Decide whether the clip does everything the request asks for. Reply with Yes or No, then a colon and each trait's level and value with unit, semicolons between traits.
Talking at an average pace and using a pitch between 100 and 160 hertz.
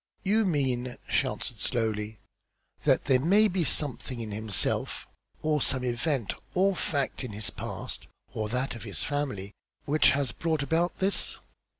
Yes: average, 155 wpm; low, 135 Hz